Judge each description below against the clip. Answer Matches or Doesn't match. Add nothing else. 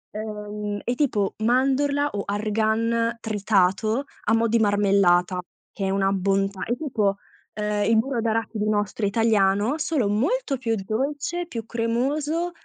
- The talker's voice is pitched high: Matches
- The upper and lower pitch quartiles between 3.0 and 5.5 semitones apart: Matches